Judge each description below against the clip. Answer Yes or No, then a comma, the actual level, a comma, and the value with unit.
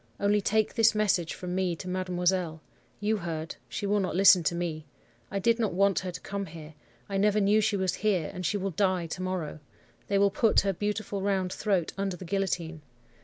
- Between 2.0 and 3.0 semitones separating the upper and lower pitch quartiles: Yes, narrow, 2.5 semitones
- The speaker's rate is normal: No, fast, 210 wpm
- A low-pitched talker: No, high, 190 Hz